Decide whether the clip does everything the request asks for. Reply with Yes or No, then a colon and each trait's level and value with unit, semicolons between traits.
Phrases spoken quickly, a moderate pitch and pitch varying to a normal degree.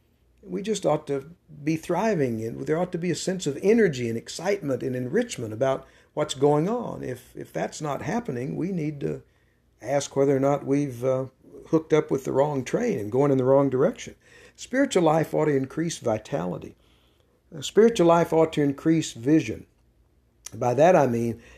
No: average, 180 wpm; medium, 145 Hz; average, 4.3 semitones